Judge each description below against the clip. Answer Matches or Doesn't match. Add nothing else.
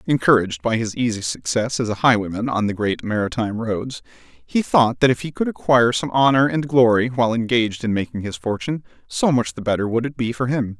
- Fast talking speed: Matches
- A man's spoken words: Matches